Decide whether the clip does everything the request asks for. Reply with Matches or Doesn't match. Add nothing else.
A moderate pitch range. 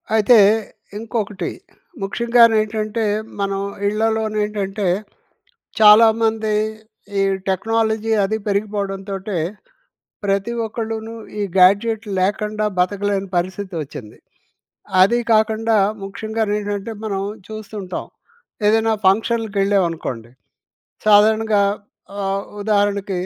Doesn't match